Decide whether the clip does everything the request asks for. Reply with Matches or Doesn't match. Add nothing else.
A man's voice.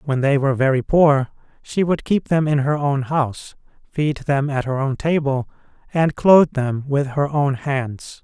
Matches